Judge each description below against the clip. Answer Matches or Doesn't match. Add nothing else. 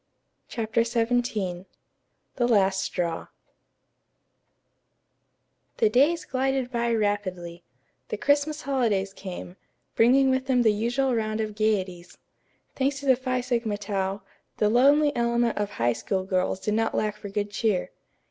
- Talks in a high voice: Matches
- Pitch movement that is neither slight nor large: Matches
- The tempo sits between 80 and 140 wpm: Matches